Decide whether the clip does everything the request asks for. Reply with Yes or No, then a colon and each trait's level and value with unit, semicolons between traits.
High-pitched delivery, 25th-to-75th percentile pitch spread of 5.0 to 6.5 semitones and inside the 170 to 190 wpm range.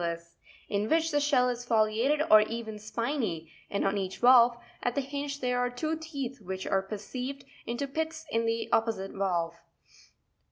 Yes: high, 235 Hz; wide, 5.4 semitones; average, 175 wpm